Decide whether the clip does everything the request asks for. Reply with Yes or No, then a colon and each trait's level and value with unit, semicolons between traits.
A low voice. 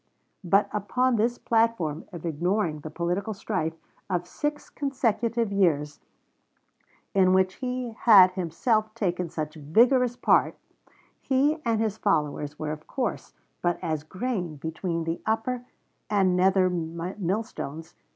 No: high, 190 Hz